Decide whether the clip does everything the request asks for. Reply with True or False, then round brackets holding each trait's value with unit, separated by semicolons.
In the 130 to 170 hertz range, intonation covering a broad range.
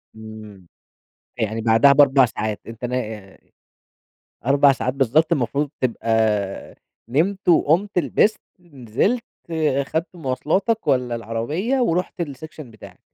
True (135 Hz; 6.0 semitones)